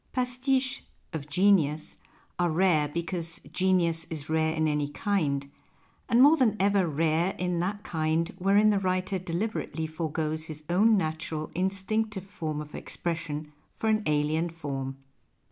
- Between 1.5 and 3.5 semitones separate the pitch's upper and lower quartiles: No, average, 3.9 semitones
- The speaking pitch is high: No, medium, 170 Hz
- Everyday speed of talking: Yes, average, 145 wpm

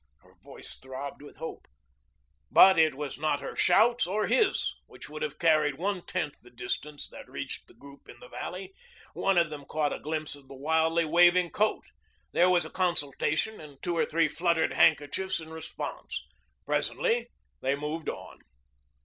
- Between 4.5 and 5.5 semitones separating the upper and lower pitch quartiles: No, average, 3.7 semitones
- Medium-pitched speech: Yes, medium, 160 Hz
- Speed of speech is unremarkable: Yes, average, 175 wpm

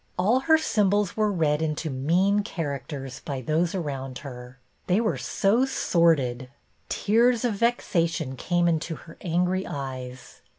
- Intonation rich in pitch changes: Yes, wide, 6.6 semitones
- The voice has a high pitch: No, medium, 170 Hz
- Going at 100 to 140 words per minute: Yes, slow, 135 wpm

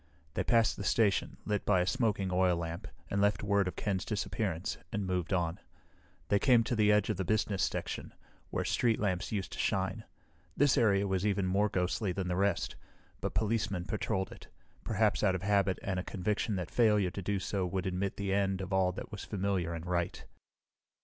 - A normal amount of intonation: No, narrow, 2.3 semitones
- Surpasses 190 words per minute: Yes, average, 200 wpm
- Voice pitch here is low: Yes, low, 100 Hz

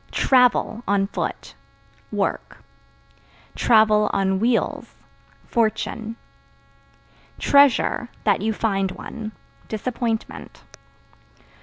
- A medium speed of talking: No, slow, 65 wpm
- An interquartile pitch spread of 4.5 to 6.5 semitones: No, narrow, 2.4 semitones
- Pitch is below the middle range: No, high, 220 Hz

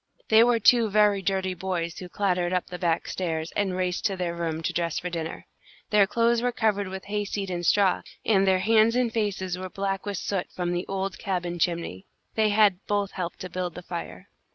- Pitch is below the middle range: No, high, 190 Hz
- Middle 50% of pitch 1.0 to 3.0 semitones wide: Yes, average, 2.7 semitones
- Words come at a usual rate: No, fast, 210 wpm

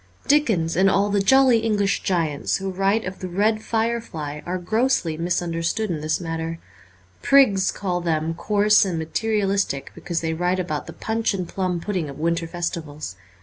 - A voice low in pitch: No, medium, 185 Hz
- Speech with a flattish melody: No, average, 4.1 semitones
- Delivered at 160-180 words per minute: Yes, average, 170 wpm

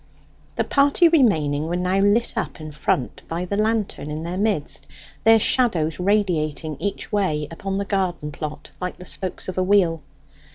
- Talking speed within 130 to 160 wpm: No, average, 170 wpm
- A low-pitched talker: No, medium, 185 Hz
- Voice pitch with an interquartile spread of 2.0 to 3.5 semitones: No, average, 4.7 semitones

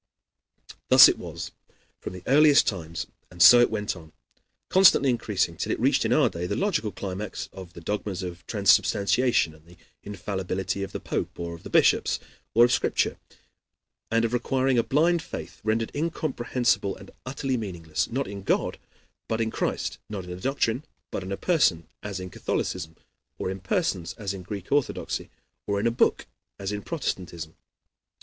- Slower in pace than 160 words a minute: No, average, 175 wpm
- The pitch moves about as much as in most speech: Yes, average, 5.0 semitones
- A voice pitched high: No, low, 100 Hz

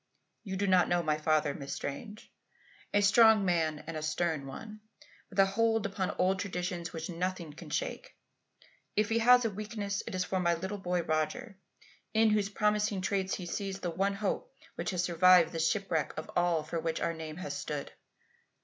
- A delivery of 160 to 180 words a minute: No, average, 190 wpm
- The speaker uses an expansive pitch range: No, average, 3.9 semitones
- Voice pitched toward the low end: No, medium, 185 Hz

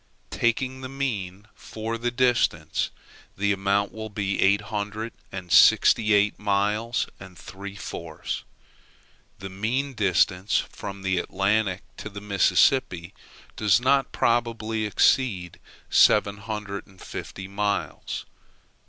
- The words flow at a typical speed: No, slow, 120 wpm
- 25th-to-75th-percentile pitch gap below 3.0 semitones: Yes, narrow, 2.6 semitones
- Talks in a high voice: No, low, 100 Hz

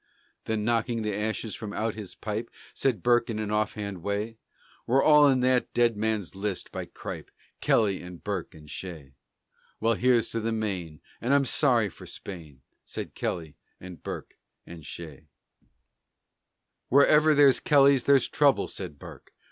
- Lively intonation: No, average, 4.4 semitones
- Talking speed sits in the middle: Yes, average, 155 wpm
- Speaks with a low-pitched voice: Yes, low, 110 Hz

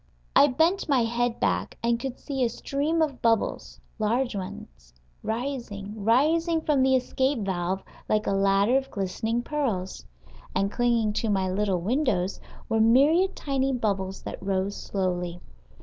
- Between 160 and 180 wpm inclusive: No, average, 150 wpm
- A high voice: Yes, high, 230 Hz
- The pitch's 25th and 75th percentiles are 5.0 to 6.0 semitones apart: Yes, wide, 5.4 semitones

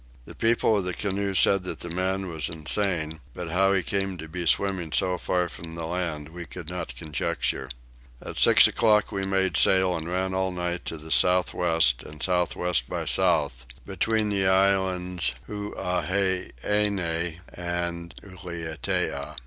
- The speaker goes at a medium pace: Yes, average, 160 wpm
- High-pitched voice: No, very low, 90 Hz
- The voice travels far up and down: No, narrow, 2.6 semitones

